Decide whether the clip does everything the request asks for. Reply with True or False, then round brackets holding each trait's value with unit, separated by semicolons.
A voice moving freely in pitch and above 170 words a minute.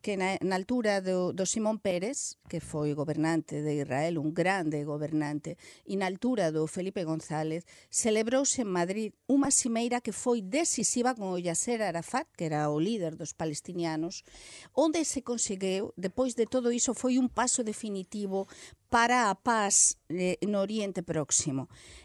False (6.2 semitones; 155 wpm)